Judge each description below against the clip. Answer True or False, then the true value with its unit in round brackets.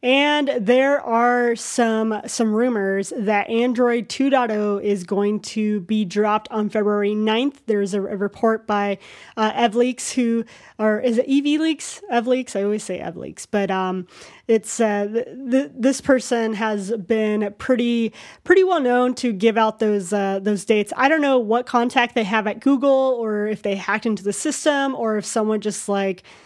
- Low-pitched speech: False (225 Hz)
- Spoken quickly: False (170 wpm)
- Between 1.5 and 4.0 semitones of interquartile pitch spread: True (3.0 semitones)